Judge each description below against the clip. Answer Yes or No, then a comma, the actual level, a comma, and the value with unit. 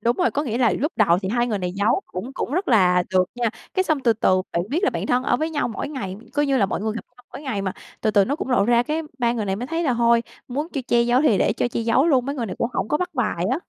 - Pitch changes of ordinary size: Yes, average, 4.9 semitones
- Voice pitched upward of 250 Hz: No, high, 240 Hz